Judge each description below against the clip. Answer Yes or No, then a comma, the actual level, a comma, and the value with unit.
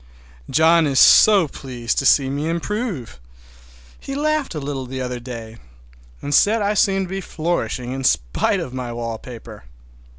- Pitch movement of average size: No, wide, 7.5 semitones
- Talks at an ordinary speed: Yes, average, 160 wpm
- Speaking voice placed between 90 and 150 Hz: Yes, medium, 140 Hz